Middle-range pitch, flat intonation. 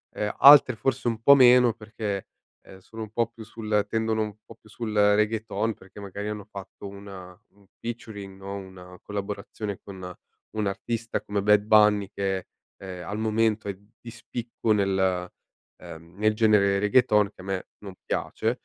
No: low, 105 Hz; narrow, 2.2 semitones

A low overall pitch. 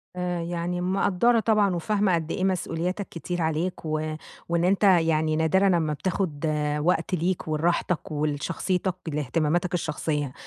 No: medium, 170 Hz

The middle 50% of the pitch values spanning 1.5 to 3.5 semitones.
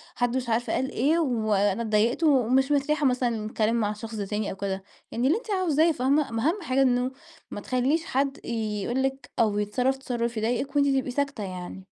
No: average, 4.1 semitones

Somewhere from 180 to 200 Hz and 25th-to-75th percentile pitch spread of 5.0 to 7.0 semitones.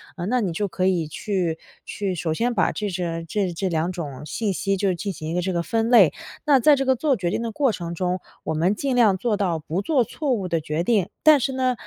Yes: high, 190 Hz; wide, 5.6 semitones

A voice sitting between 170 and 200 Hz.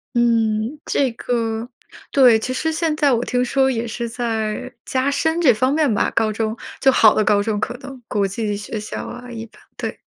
No: high, 235 Hz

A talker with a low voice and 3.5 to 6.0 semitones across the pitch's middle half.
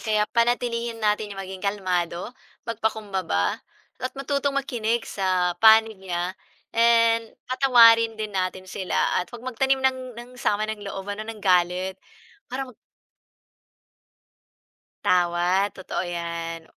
No: high, 215 Hz; average, 4.0 semitones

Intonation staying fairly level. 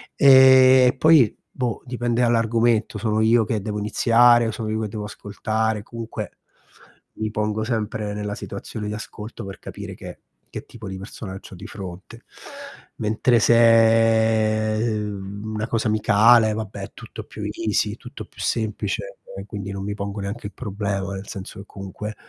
Yes: narrow, 2.0 semitones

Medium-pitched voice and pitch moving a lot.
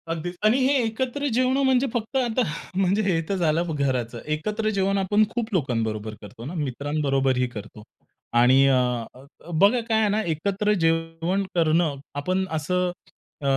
Yes: medium, 175 Hz; wide, 7.2 semitones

